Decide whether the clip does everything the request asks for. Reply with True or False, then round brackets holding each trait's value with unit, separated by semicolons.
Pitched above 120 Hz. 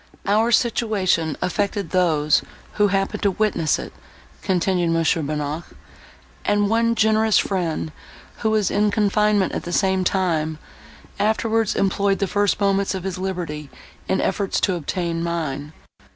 True (190 Hz)